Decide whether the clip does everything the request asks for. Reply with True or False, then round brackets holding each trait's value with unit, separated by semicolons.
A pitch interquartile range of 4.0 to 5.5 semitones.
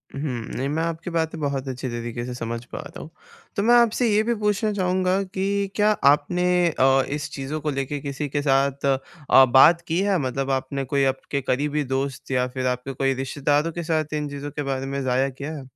False (3.6 semitones)